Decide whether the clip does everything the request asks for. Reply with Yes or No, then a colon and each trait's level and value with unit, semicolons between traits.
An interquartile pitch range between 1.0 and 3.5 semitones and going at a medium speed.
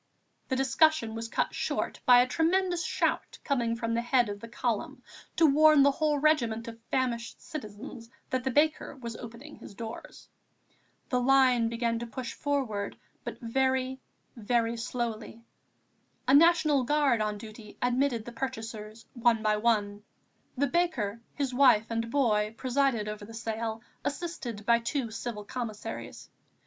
Yes: average, 3.2 semitones; average, 150 wpm